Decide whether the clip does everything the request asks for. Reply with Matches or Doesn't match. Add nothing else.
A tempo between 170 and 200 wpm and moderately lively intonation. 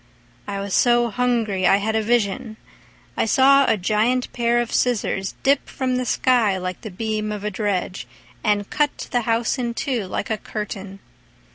Matches